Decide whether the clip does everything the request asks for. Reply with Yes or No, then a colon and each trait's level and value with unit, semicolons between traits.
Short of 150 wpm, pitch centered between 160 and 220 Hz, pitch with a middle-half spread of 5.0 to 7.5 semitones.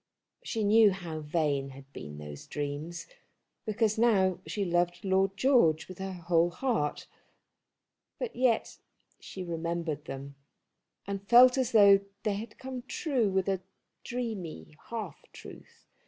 Yes: slow, 135 wpm; high, 190 Hz; wide, 5.5 semitones